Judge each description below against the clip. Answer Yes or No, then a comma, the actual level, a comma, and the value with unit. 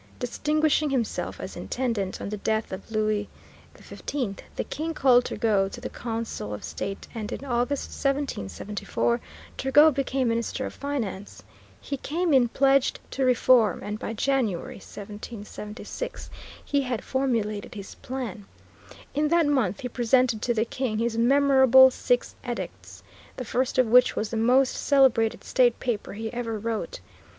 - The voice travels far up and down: No, average, 3.8 semitones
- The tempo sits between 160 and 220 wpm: No, average, 150 wpm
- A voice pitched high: Yes, high, 245 Hz